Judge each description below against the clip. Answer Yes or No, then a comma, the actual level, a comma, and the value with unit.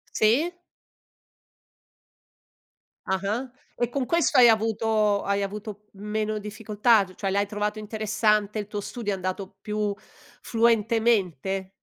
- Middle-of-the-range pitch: No, high, 210 Hz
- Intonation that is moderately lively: No, narrow, 1.8 semitones